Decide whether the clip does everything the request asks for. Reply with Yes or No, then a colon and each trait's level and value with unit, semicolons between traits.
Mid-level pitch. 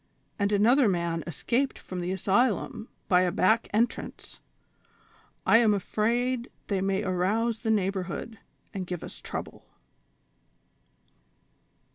No: high, 200 Hz